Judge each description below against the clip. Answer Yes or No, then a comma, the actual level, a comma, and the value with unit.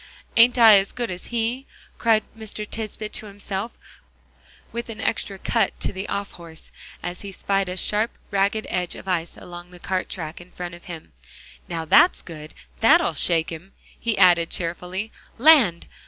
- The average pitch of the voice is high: Yes, high, 195 Hz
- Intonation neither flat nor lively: Yes, average, 3.9 semitones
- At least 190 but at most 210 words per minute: No, average, 170 wpm